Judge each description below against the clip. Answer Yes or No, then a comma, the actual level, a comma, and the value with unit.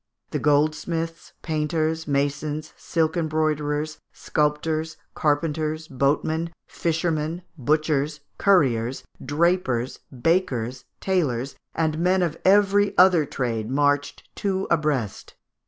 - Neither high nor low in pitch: Yes, medium, 155 Hz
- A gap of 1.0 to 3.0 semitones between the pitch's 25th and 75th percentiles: Yes, narrow, 2.5 semitones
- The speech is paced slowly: Yes, slow, 90 wpm